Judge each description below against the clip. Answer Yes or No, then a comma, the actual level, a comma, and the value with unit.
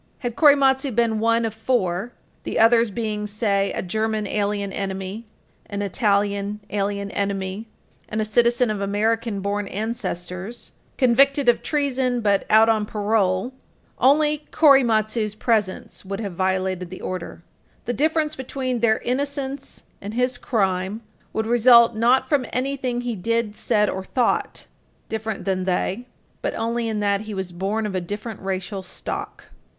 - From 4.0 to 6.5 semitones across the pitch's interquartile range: No, average, 3.3 semitones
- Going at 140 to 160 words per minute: Yes, average, 145 wpm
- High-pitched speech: Yes, high, 220 Hz